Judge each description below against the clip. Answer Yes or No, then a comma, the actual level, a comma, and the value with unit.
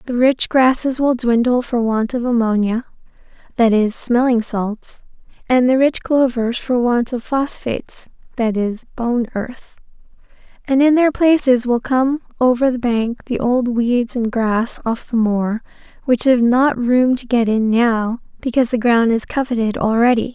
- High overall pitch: Yes, high, 240 Hz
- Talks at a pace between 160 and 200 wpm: Yes, average, 165 wpm